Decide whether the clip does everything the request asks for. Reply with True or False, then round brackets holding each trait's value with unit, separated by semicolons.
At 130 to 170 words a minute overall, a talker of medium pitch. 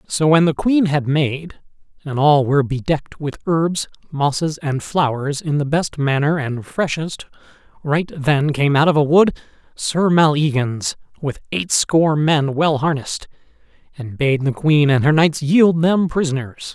True (160 wpm; 150 Hz)